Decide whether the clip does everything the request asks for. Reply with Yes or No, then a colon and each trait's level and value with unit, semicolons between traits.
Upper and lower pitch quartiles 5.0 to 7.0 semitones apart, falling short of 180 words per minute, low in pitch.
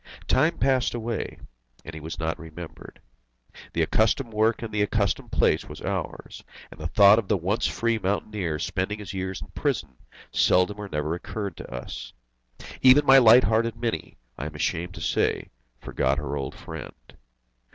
Yes: wide, 5.5 semitones; average, 170 wpm; low, 100 Hz